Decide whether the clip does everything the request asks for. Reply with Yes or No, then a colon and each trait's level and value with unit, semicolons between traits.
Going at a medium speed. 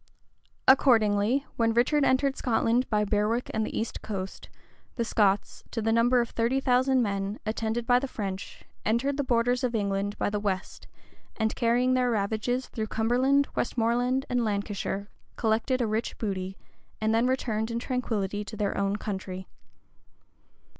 Yes: average, 155 wpm